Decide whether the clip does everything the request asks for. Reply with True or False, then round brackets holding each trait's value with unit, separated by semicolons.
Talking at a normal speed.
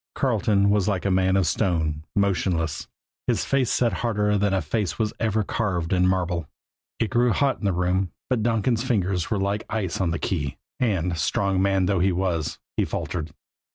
True (185 wpm)